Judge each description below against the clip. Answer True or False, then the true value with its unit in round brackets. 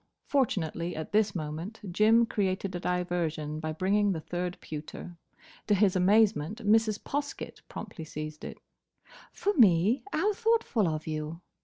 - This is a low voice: False (185 Hz)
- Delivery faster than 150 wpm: False (140 wpm)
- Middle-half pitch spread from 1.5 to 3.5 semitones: False (5.4 semitones)